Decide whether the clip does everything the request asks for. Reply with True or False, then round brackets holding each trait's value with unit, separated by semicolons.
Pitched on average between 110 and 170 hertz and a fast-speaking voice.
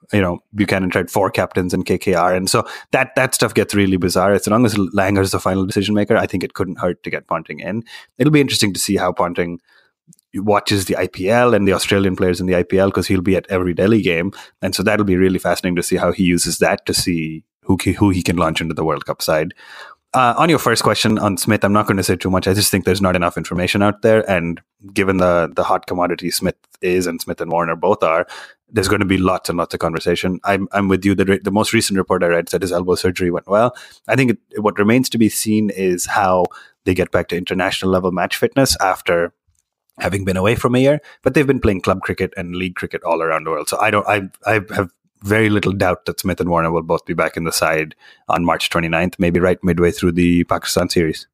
False (95 Hz; 250 wpm)